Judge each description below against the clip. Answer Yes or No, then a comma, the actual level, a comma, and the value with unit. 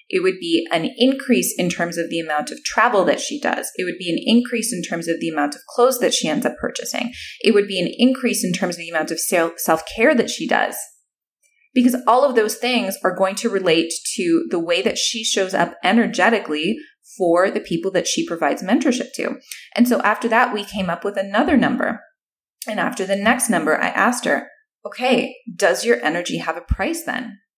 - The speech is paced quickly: Yes, fast, 215 wpm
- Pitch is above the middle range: Yes, high, 220 Hz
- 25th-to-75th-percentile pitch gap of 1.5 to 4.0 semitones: No, wide, 5.6 semitones